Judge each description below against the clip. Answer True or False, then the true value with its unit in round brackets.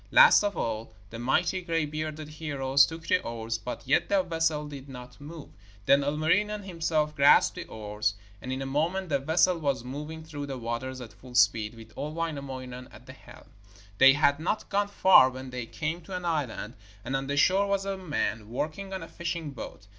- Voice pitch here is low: False (145 Hz)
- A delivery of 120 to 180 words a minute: False (200 wpm)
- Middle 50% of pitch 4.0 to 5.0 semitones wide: True (4.3 semitones)